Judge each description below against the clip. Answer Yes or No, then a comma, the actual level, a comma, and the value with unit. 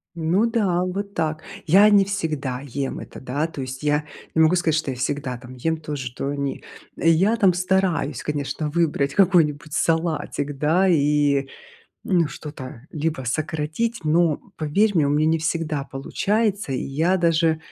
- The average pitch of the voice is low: No, medium, 155 Hz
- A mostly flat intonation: No, average, 3.6 semitones